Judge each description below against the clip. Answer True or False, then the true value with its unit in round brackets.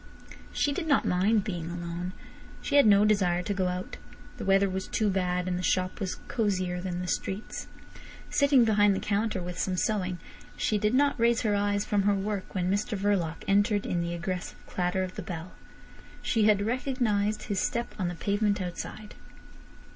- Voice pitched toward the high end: True (200 Hz)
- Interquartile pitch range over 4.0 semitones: False (2.7 semitones)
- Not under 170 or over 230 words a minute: True (185 wpm)